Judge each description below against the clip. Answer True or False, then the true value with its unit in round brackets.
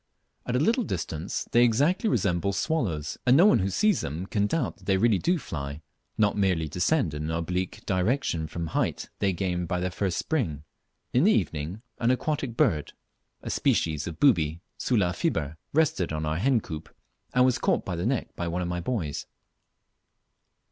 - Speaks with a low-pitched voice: True (95 Hz)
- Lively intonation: True (7.1 semitones)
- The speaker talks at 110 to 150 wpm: False (190 wpm)